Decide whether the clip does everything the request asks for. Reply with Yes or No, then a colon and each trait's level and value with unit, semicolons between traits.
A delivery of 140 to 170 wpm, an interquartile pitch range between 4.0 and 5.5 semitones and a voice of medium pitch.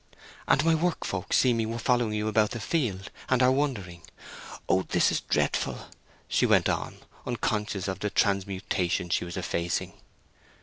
No: average, 150 wpm; average, 4.7 semitones; low, 105 Hz